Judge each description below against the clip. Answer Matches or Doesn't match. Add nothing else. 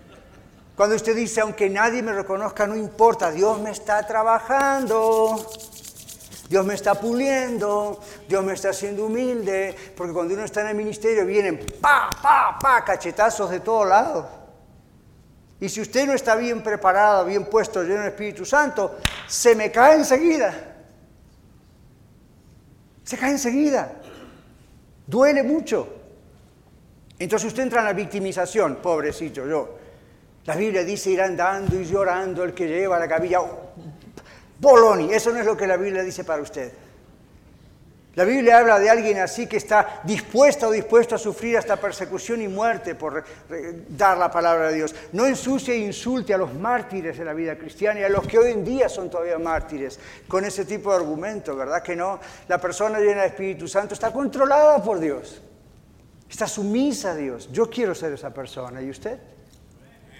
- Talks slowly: Doesn't match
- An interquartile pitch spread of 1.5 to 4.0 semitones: Matches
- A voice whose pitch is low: Doesn't match